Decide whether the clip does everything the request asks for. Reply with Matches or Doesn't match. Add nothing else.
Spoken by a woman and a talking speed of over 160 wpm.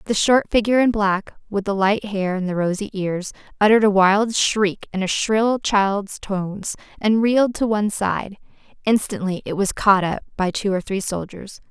Matches